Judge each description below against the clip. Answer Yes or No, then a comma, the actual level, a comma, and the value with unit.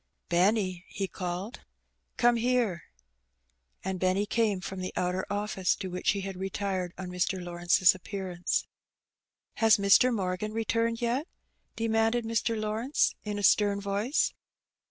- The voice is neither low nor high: No, high, 200 Hz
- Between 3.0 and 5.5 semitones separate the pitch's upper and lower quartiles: Yes, average, 3.4 semitones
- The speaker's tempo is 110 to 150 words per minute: Yes, average, 140 wpm